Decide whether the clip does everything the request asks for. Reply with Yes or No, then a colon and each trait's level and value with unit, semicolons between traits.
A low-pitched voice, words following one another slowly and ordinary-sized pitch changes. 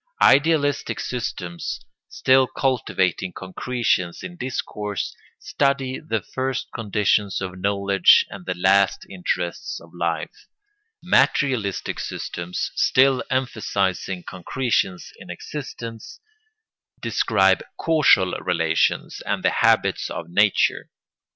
No: low, 100 Hz; slow, 95 wpm; wide, 6.0 semitones